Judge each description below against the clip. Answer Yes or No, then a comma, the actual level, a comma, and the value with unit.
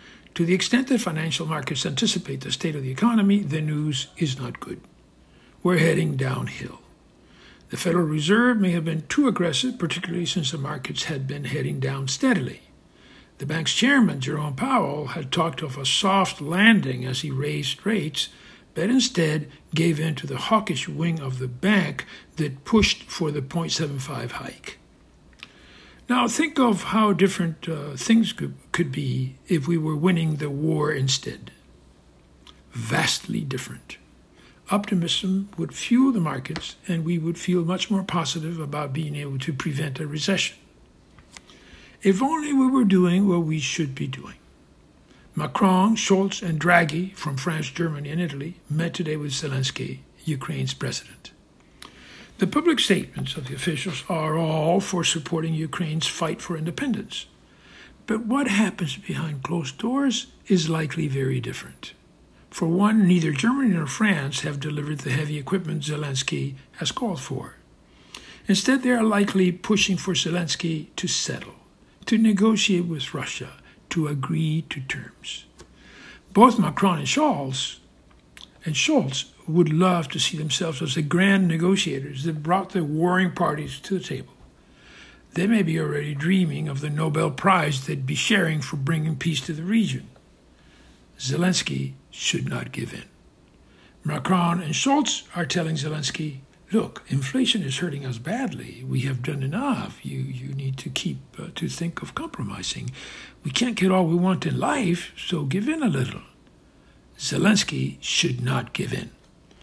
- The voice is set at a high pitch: No, medium, 165 Hz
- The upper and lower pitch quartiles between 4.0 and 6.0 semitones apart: Yes, average, 4.6 semitones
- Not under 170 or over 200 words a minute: No, average, 150 wpm